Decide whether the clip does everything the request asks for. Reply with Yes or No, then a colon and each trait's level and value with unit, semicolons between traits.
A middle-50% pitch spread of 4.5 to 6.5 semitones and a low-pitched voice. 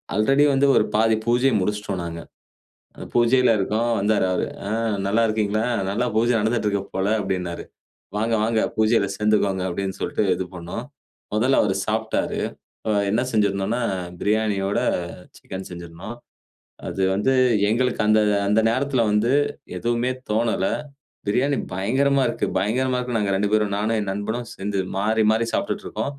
No: average, 3.1 semitones; low, 110 Hz